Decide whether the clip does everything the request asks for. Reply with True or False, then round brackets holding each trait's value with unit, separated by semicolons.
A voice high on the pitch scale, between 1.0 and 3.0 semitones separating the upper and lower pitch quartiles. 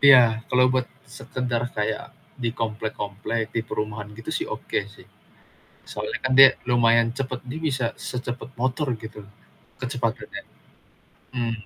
False (120 Hz; 2.4 semitones)